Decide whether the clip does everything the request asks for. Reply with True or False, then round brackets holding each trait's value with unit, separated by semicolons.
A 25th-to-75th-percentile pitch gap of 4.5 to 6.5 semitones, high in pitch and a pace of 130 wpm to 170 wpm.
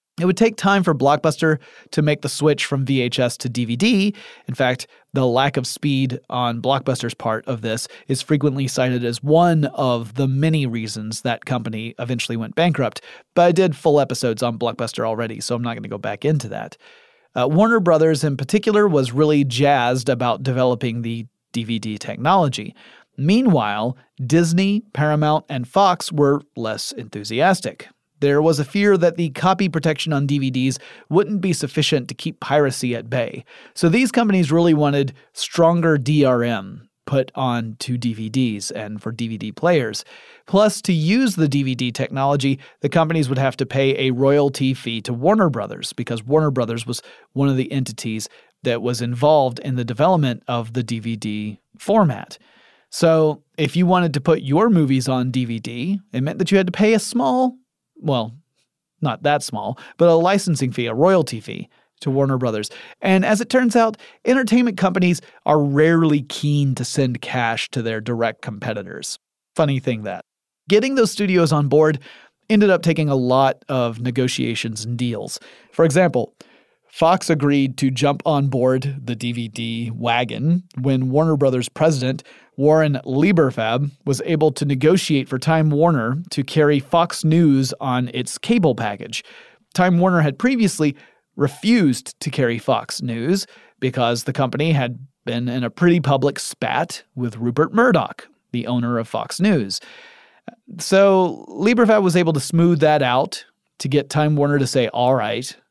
False (5.0 semitones; 140 Hz; 165 wpm)